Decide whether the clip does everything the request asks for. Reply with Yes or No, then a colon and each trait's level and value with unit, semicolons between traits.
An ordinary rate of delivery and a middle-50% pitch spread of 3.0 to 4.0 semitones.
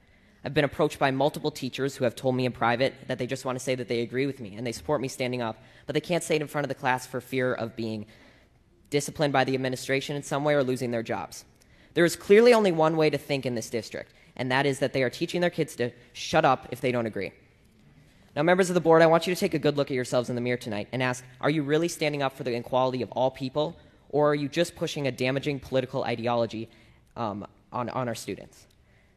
No: fast, 260 wpm; average, 3.4 semitones